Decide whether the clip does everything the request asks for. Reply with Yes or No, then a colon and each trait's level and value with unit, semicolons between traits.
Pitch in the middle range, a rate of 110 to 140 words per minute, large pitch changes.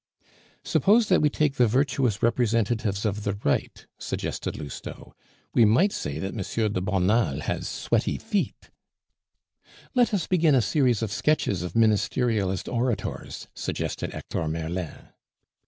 No: low, 115 Hz; slow, 135 wpm; wide, 5.8 semitones